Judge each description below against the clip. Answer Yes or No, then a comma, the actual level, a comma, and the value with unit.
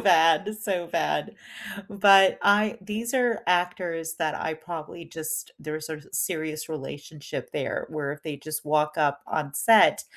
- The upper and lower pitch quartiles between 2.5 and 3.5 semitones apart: No, average, 3.9 semitones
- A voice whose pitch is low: No, medium, 160 Hz